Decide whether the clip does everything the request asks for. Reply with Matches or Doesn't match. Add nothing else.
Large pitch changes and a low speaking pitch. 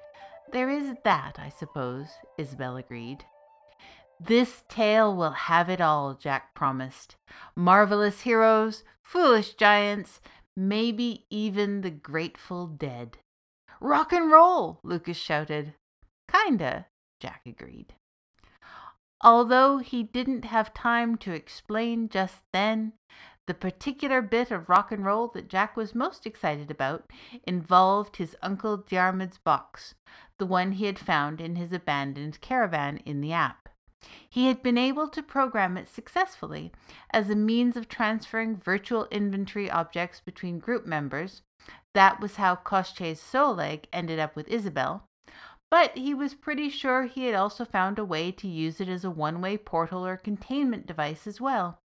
Doesn't match